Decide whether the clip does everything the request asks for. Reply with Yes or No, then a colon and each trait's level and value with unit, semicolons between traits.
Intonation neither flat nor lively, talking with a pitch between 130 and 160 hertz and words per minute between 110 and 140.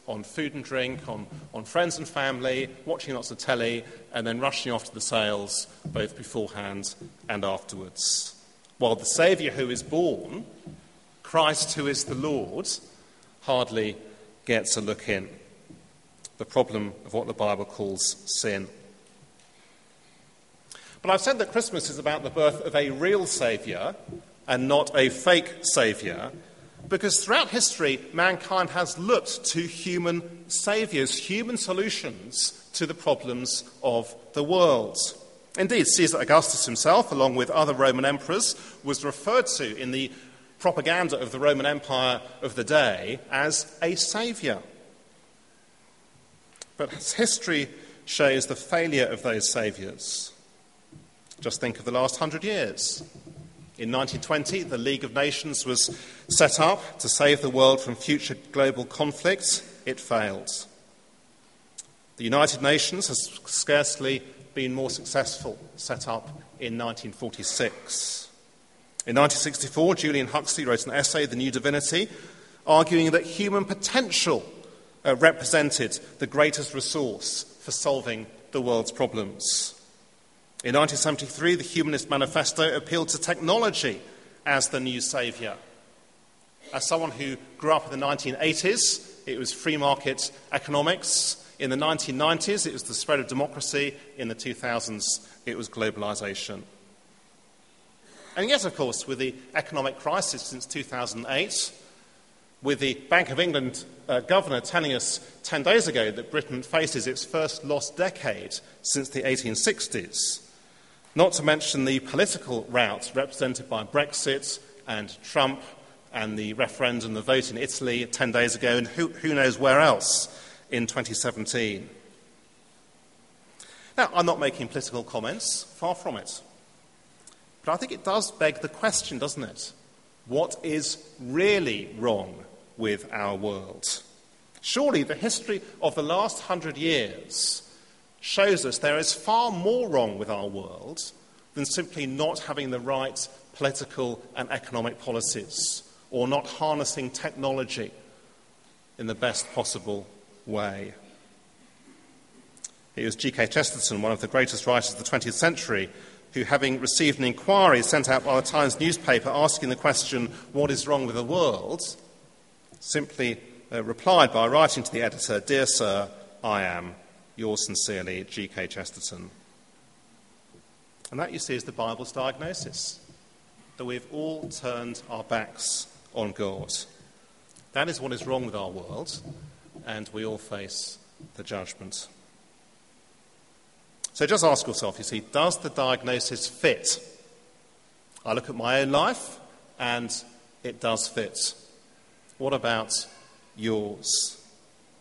Yes: average, 4.7 semitones; medium, 140 Hz; slow, 135 wpm